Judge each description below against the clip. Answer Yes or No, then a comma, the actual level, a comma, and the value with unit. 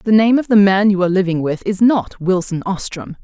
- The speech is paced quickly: Yes, fast, 240 wpm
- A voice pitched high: Yes, high, 195 Hz